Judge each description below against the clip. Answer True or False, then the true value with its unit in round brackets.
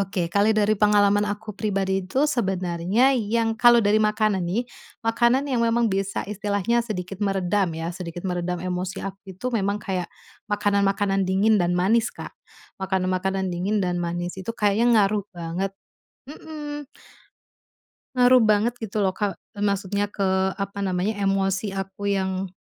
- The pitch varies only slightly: True (2.3 semitones)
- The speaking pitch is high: True (200 Hz)